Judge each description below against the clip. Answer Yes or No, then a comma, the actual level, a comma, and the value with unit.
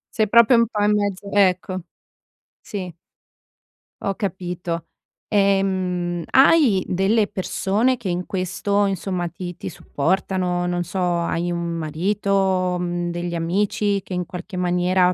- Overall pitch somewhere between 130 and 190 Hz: Yes, medium, 185 Hz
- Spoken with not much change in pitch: Yes, narrow, 2.2 semitones